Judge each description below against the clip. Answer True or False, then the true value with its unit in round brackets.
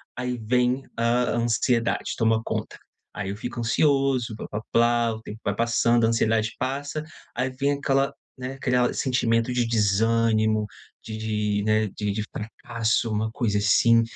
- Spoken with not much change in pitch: True (2.2 semitones)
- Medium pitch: False (115 Hz)